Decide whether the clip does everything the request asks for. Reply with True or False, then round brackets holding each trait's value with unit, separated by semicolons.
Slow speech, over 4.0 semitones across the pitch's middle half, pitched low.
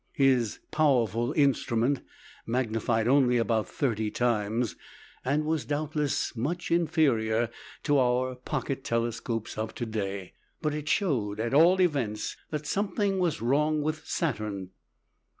True (125 wpm; 5.0 semitones; 130 Hz)